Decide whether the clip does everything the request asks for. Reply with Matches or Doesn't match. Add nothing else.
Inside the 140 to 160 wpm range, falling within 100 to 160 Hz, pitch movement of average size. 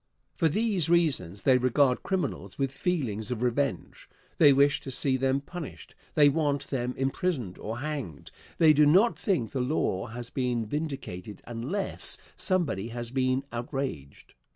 Matches